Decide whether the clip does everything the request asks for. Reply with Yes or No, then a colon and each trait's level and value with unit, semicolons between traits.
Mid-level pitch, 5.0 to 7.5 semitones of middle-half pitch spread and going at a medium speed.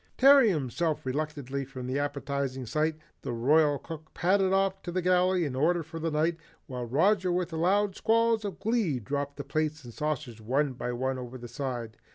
Yes: medium, 150 Hz; wide, 5.4 semitones; average, 195 wpm